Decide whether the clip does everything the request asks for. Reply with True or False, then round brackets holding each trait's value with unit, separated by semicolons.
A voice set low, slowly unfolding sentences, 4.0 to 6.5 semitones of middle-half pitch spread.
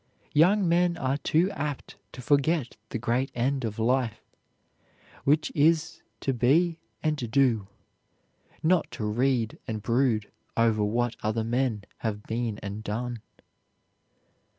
True (125 Hz; 130 wpm; 5.0 semitones)